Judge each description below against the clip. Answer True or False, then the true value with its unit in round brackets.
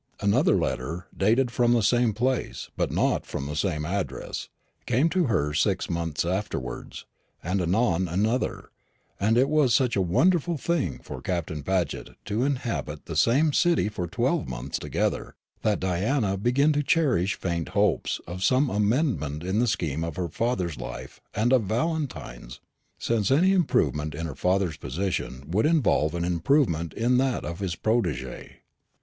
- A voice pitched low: True (100 Hz)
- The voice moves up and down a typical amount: False (7.0 semitones)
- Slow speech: False (160 wpm)